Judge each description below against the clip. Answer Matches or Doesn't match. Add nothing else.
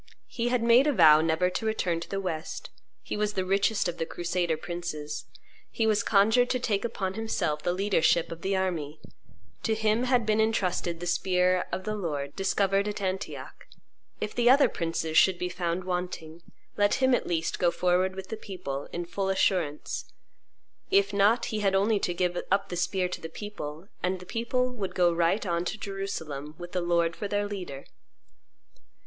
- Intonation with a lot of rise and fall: Doesn't match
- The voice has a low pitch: Doesn't match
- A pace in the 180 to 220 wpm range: Matches